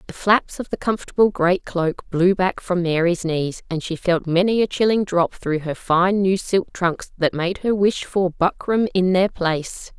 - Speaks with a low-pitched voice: No, medium, 180 Hz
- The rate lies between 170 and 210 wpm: Yes, fast, 205 wpm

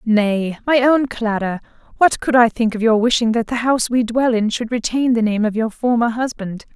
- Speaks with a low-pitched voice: No, high, 230 Hz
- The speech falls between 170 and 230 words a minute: Yes, fast, 205 wpm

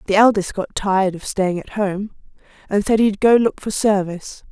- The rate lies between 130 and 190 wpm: No, average, 200 wpm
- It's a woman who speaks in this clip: Yes, female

